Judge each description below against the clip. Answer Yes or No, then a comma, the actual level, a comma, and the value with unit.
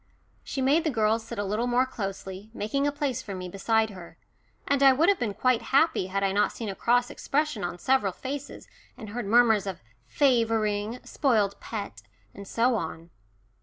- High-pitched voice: Yes, high, 225 Hz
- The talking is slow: No, average, 190 wpm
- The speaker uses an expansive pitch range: No, average, 4.5 semitones